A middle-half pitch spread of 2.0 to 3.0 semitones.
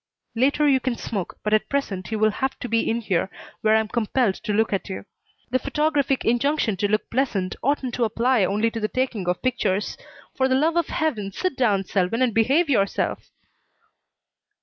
No: average, 4.1 semitones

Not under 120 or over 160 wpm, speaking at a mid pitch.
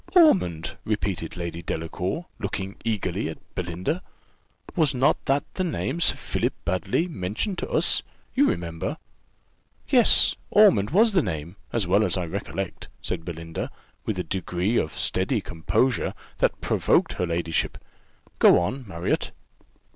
No: average, 140 wpm; very low, 95 Hz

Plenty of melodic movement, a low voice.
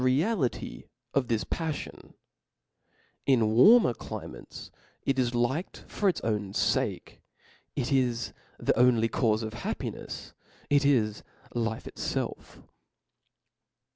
No: average, 3.7 semitones; low, 120 Hz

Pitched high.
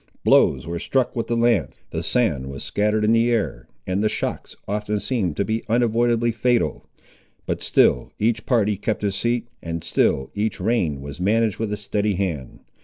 No: low, 105 Hz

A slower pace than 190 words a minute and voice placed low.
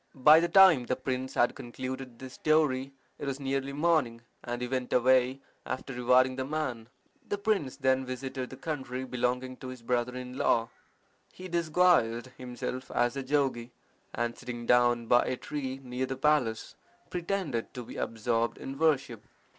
Yes: average, 165 wpm; low, 130 Hz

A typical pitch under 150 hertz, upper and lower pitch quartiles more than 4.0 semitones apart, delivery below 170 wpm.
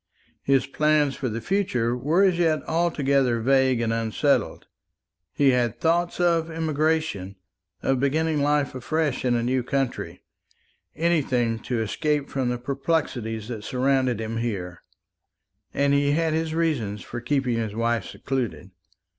Yes: low, 135 Hz; average, 4.8 semitones; average, 140 wpm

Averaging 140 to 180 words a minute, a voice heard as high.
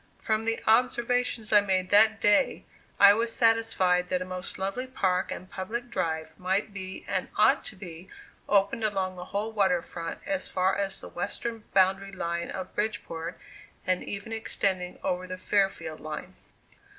Yes: average, 160 wpm; high, 195 Hz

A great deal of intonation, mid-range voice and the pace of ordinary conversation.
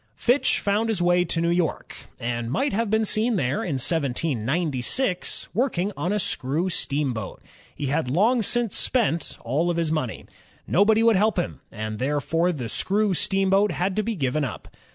Yes: wide, 6.7 semitones; medium, 175 Hz; average, 175 wpm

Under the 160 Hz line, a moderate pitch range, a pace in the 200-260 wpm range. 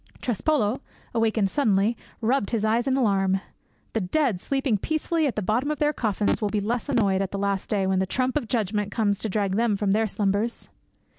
No: high, 215 Hz; average, 3.8 semitones; fast, 205 wpm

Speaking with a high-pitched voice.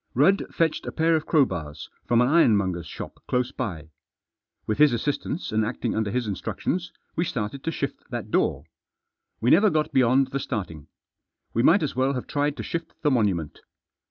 No: low, 125 Hz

